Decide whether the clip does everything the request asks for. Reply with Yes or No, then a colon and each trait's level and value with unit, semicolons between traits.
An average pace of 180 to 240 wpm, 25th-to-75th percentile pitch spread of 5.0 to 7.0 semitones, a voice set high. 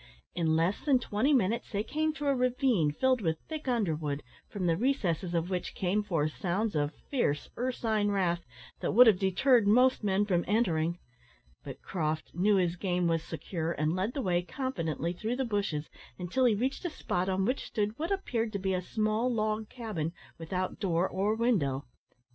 Yes: average, 185 wpm; wide, 5.6 semitones; high, 200 Hz